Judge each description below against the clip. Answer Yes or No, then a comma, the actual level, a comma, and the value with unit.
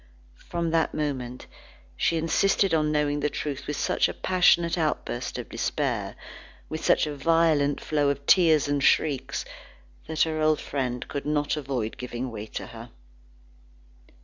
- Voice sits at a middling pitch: Yes, medium, 150 Hz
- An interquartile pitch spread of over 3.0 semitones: No, narrow, 2.5 semitones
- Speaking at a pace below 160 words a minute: Yes, average, 150 wpm